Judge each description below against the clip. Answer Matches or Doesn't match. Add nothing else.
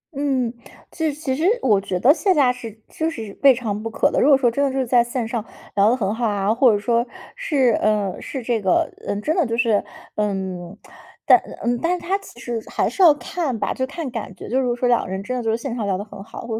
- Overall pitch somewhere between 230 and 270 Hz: Matches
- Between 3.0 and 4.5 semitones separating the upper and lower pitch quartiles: Matches